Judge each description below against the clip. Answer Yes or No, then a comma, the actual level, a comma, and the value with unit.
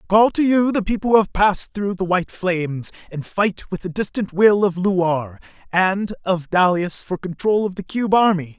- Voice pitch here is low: No, high, 190 Hz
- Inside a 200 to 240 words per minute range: Yes, fast, 205 wpm